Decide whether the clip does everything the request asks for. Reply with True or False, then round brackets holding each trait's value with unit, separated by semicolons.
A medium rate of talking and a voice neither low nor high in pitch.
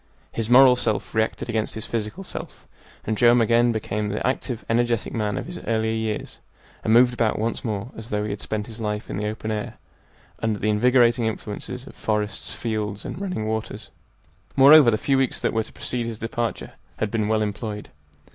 False (195 wpm; 110 Hz)